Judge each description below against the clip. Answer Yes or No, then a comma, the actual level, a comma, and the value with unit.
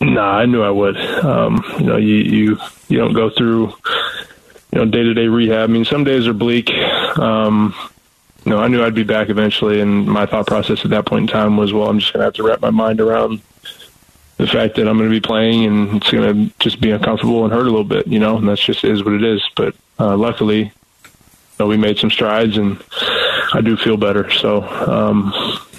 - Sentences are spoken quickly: Yes, fast, 230 wpm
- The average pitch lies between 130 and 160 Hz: No, low, 110 Hz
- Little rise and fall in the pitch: Yes, narrow, 1.3 semitones